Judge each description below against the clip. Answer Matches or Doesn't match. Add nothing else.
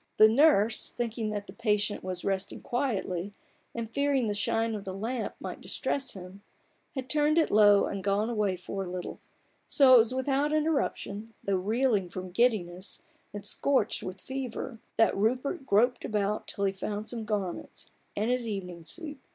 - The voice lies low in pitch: Doesn't match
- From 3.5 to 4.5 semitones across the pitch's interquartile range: Matches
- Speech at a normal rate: Matches